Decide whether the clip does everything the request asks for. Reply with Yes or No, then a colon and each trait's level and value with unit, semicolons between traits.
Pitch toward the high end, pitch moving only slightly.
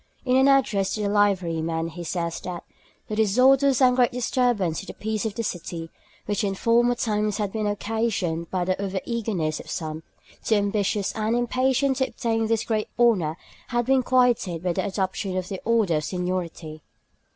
No: high, 205 Hz; average, 4.6 semitones